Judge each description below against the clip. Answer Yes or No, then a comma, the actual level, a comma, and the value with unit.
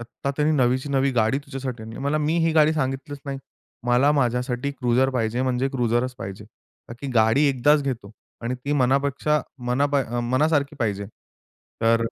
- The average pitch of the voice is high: No, low, 130 Hz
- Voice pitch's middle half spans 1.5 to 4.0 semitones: Yes, average, 2.9 semitones